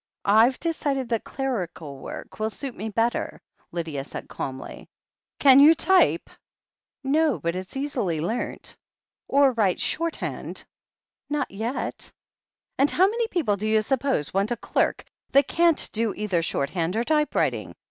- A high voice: Yes, high, 235 Hz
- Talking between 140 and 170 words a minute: Yes, average, 145 wpm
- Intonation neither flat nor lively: No, wide, 6.7 semitones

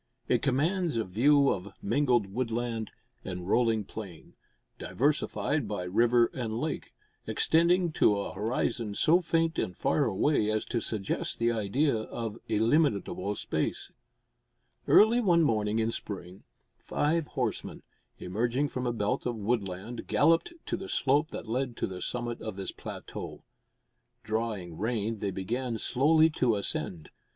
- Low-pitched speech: Yes, low, 115 Hz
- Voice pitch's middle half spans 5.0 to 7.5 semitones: Yes, wide, 5.4 semitones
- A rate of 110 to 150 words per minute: Yes, average, 140 wpm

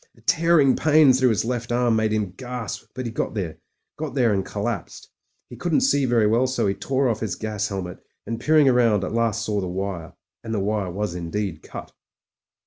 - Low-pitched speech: Yes, low, 115 Hz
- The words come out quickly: Yes, fast, 215 wpm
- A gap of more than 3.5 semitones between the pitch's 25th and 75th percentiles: Yes, average, 4.1 semitones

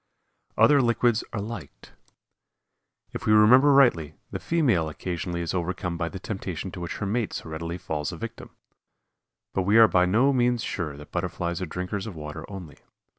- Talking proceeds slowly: No, average, 175 wpm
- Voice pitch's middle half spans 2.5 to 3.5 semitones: No, average, 5.0 semitones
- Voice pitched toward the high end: No, very low, 95 Hz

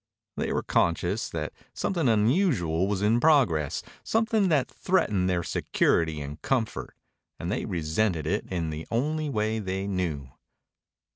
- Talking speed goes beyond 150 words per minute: No, average, 140 wpm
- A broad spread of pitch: Yes, wide, 8.2 semitones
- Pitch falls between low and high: No, low, 100 Hz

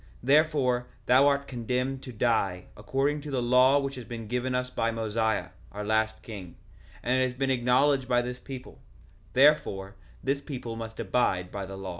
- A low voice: Yes, low, 125 Hz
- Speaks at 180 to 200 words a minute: Yes, average, 185 wpm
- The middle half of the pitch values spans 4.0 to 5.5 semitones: No, average, 3.3 semitones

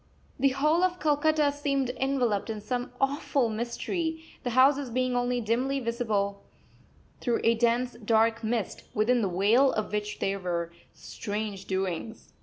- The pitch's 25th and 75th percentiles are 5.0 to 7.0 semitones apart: No, average, 4.1 semitones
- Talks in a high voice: Yes, high, 240 Hz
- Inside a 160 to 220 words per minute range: No, average, 145 wpm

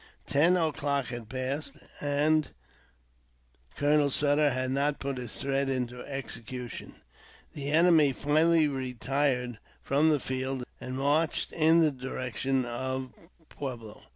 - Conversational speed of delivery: No, slow, 120 wpm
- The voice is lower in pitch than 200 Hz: Yes, low, 135 Hz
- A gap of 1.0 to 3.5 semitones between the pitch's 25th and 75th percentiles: Yes, narrow, 2.4 semitones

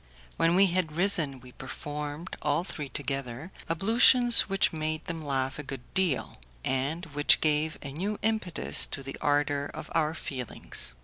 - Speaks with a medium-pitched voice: Yes, medium, 150 Hz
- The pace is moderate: Yes, average, 160 wpm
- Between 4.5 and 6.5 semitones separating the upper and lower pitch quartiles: No, average, 4.1 semitones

